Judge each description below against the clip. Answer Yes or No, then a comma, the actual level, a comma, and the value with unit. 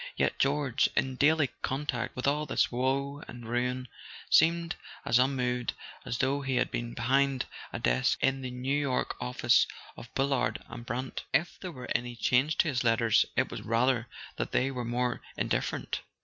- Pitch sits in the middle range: No, low, 130 Hz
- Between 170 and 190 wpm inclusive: Yes, average, 175 wpm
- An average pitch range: No, narrow, 2.2 semitones